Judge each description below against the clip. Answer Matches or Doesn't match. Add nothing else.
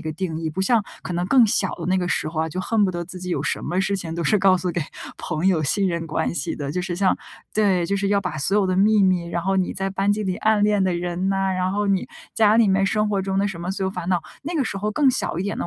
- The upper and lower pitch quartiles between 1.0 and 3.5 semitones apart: Matches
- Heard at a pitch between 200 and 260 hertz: Doesn't match